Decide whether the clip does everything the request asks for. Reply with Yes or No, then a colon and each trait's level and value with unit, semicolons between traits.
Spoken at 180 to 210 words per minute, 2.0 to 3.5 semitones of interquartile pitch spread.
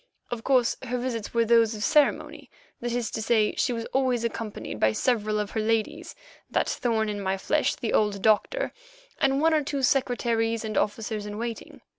Yes: average, 185 wpm; average, 3.0 semitones